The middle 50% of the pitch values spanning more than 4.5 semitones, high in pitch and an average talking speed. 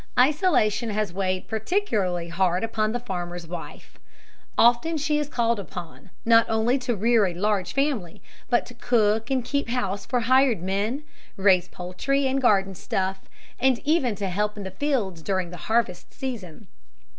Yes: average, 5.0 semitones; high, 215 Hz; average, 160 wpm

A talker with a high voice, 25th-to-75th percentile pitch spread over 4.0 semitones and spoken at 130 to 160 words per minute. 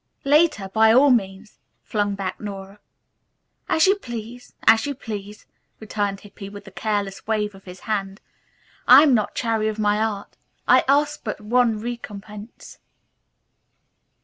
No: high, 215 Hz; average, 2.8 semitones; average, 150 wpm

